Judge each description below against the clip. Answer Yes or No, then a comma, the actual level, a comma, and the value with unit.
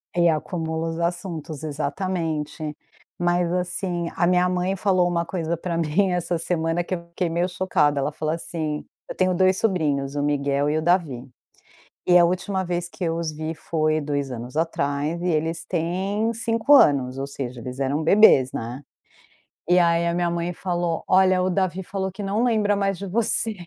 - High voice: No, medium, 170 Hz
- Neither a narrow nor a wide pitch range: Yes, average, 3.1 semitones